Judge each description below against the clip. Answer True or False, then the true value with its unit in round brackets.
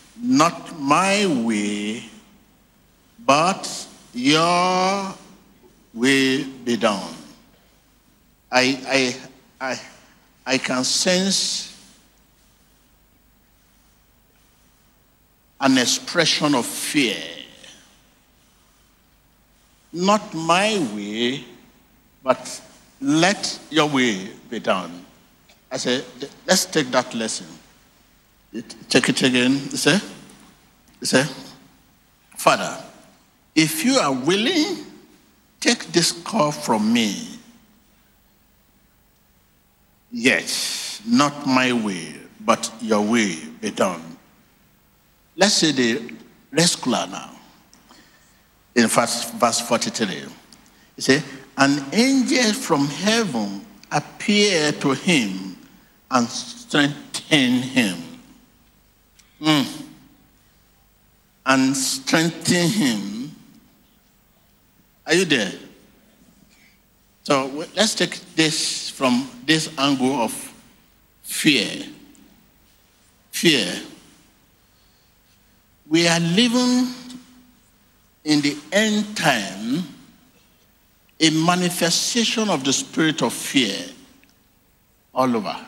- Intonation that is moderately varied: False (8.1 semitones)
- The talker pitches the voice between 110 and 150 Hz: False (160 Hz)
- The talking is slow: True (80 wpm)